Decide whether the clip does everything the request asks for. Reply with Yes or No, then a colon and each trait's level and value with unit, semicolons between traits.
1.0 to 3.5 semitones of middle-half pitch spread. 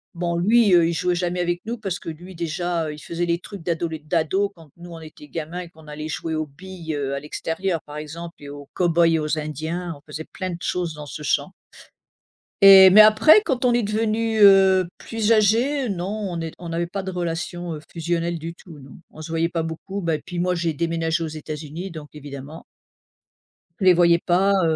Yes: average, 2.9 semitones